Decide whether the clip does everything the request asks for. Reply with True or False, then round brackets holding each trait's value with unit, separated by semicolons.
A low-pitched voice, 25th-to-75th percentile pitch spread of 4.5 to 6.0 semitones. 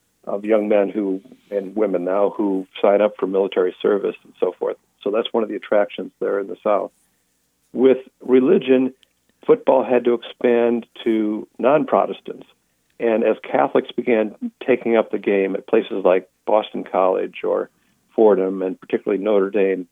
True (110 Hz; 5.2 semitones)